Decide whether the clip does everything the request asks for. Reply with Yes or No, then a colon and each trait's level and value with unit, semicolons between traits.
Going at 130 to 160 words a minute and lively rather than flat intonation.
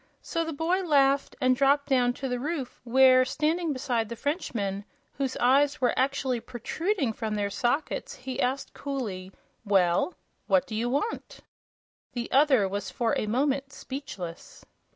No: average, 150 wpm; average, 3.4 semitones